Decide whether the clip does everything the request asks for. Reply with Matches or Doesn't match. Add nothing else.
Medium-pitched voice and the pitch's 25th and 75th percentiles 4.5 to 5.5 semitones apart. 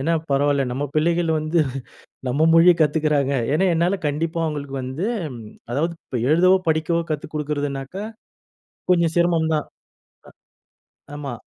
Doesn't match